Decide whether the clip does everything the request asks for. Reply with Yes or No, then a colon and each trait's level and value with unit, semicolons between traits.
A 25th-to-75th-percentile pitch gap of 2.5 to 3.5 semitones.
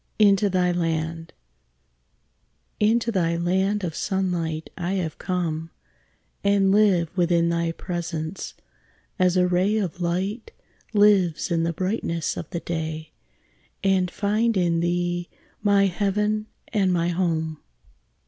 Yes: average, 2.9 semitones